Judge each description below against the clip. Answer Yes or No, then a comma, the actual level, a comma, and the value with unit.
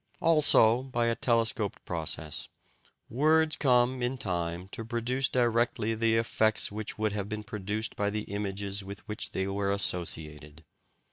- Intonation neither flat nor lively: Yes, average, 3.3 semitones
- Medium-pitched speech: No, low, 110 Hz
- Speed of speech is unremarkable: Yes, average, 145 wpm